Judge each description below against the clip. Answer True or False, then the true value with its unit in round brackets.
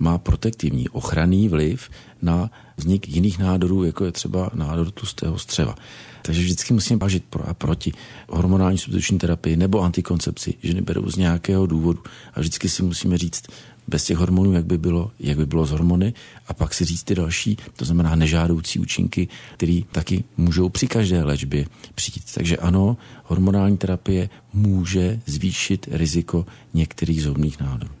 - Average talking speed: True (160 wpm)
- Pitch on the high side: False (90 Hz)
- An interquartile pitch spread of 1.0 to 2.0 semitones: False (2.5 semitones)